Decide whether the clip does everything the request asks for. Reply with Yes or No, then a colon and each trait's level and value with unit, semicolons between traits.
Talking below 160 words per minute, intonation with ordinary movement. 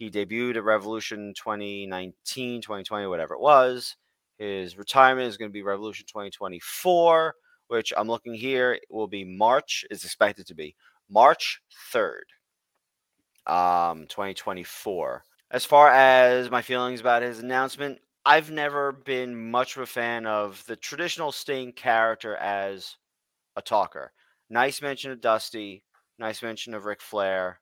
Yes: average, 140 wpm; average, 4.0 semitones